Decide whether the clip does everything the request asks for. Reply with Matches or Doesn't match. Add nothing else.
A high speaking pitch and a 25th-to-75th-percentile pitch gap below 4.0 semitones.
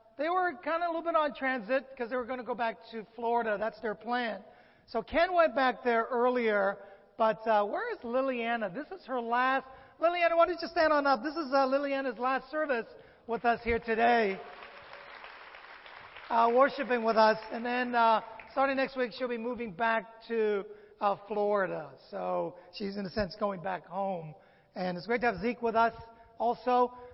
Matches